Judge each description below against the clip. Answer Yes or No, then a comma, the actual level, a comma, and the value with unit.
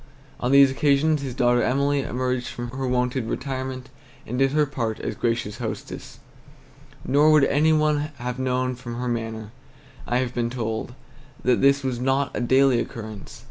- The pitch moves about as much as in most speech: No, narrow, 2.3 semitones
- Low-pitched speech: Yes, low, 130 Hz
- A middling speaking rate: Yes, average, 170 wpm